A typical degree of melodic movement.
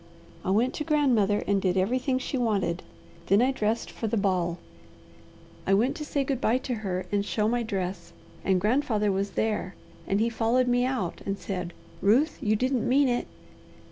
Yes: average, 4.4 semitones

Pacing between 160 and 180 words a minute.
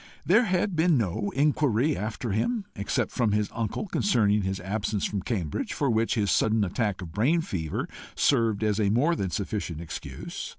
Yes: average, 170 wpm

